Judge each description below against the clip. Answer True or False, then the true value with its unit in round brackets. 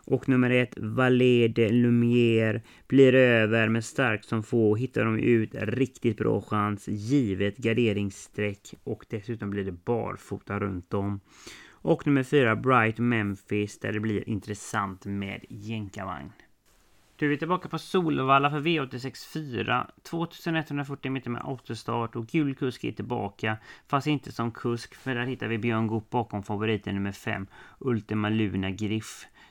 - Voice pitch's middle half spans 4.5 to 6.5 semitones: False (3.7 semitones)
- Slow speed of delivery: False (150 wpm)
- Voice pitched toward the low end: True (115 Hz)